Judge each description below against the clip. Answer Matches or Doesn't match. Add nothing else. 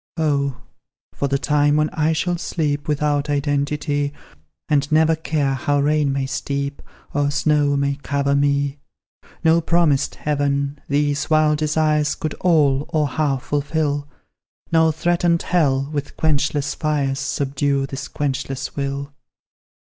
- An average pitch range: Doesn't match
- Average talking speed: Doesn't match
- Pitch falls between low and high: Matches